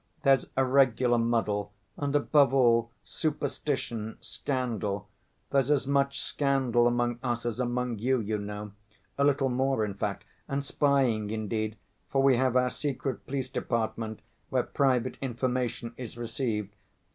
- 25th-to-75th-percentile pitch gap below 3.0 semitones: No, average, 3.3 semitones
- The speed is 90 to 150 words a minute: Yes, average, 140 wpm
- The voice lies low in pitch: Yes, low, 125 Hz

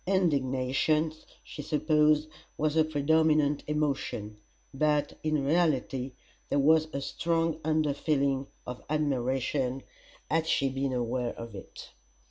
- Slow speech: Yes, slow, 115 wpm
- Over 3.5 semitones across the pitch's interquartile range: No, average, 2.7 semitones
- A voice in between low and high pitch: Yes, medium, 145 Hz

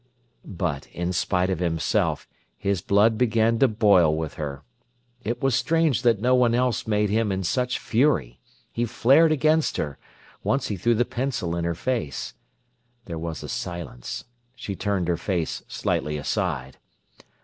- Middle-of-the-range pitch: No, low, 100 Hz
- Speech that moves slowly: No, average, 160 wpm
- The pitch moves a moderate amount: No, wide, 6.3 semitones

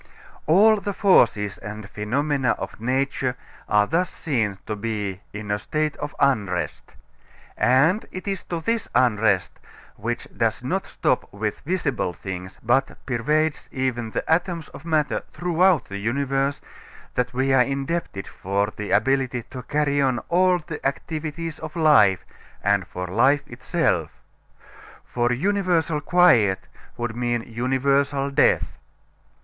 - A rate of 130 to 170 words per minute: Yes, slow, 135 wpm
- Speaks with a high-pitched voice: No, low, 135 Hz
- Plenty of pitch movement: Yes, wide, 6.2 semitones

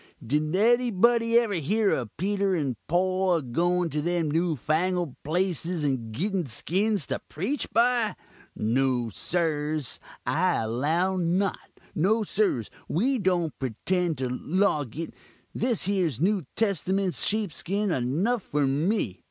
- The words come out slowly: Yes, slow, 125 wpm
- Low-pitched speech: No, medium, 175 Hz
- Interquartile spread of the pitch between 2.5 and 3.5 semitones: No, average, 5.2 semitones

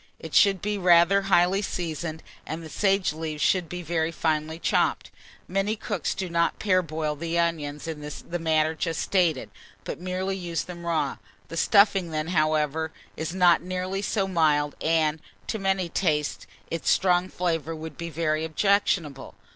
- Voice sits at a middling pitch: Yes, medium, 170 Hz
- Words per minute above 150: Yes, average, 160 wpm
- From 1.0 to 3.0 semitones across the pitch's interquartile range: Yes, average, 2.7 semitones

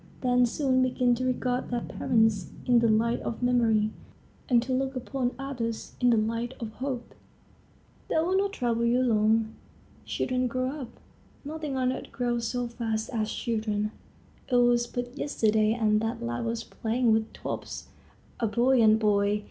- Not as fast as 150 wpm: No, average, 165 wpm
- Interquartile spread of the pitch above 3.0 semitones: No, narrow, 2.4 semitones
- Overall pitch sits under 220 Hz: No, high, 240 Hz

